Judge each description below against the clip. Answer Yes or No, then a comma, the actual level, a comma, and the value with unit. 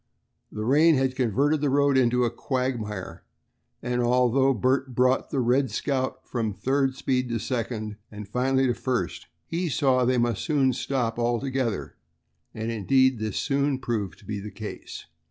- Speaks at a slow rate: No, average, 165 wpm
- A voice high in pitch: No, low, 125 Hz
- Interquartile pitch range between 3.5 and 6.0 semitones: No, average, 2.7 semitones